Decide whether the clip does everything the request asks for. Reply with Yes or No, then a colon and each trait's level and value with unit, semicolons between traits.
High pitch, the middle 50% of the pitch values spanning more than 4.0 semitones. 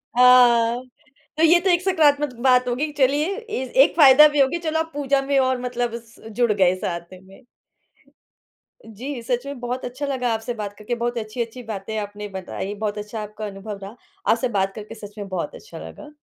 Yes: high, 240 Hz; average, 4.6 semitones